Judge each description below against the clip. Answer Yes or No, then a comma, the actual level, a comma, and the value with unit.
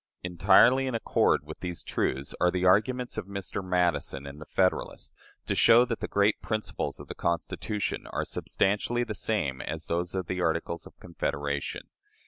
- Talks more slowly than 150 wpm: No, average, 170 wpm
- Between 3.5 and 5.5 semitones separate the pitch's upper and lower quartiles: Yes, average, 4.2 semitones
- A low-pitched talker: Yes, very low, 90 Hz